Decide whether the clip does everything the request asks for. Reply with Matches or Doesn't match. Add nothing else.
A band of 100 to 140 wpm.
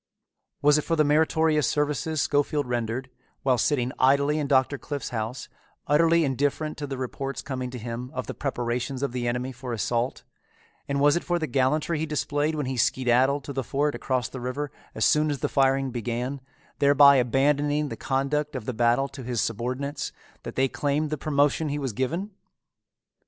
Doesn't match